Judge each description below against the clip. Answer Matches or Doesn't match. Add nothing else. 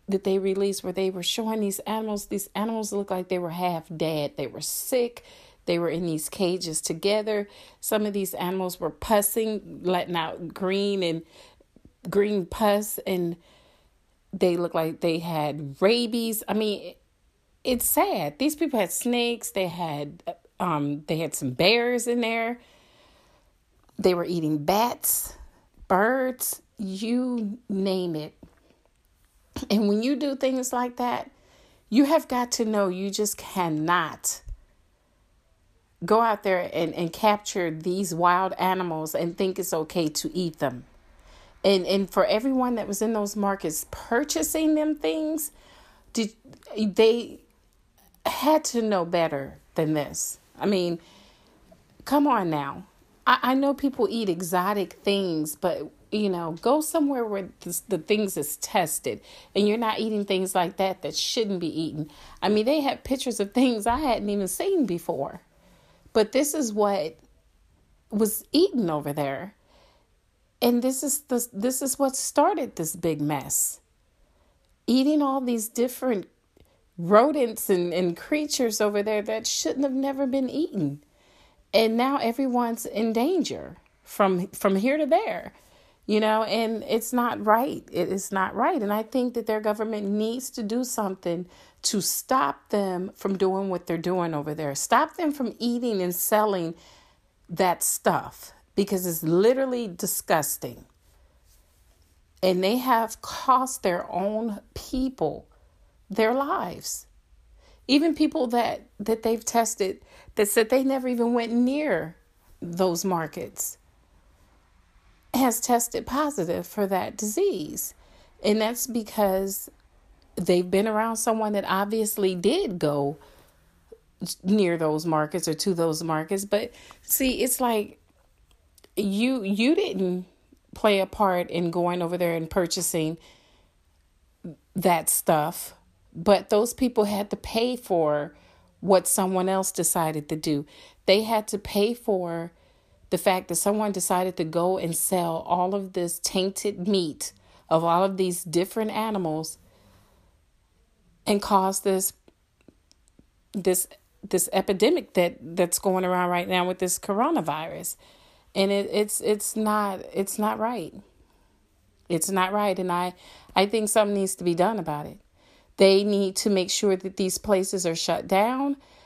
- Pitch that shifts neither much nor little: Matches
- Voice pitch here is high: Matches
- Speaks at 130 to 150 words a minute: Matches